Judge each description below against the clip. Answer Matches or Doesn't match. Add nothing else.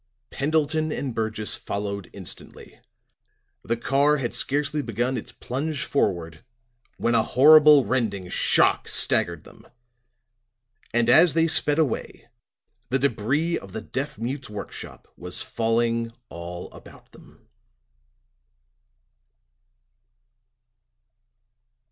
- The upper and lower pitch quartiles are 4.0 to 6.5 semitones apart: Matches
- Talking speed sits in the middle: Doesn't match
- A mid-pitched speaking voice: Doesn't match